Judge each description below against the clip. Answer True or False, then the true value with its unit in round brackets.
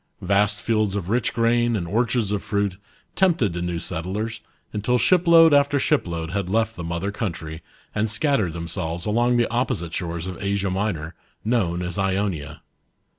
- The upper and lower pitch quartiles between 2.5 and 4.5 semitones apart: False (5.1 semitones)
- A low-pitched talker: True (100 Hz)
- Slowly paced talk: False (160 wpm)